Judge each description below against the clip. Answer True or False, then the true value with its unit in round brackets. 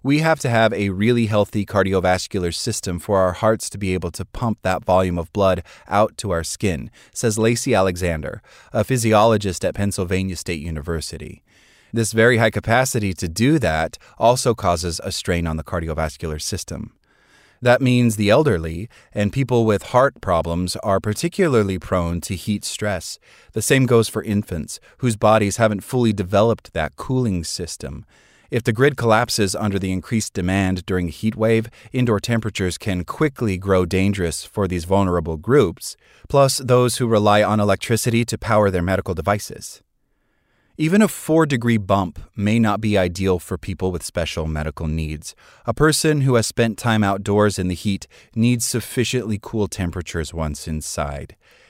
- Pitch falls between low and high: False (105 Hz)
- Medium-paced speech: True (165 wpm)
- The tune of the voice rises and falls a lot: False (4.0 semitones)